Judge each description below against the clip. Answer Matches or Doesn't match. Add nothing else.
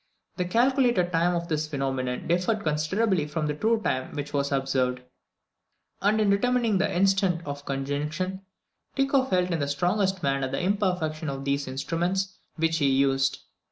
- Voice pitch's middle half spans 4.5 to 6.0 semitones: Matches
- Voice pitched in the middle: Matches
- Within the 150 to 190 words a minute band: Matches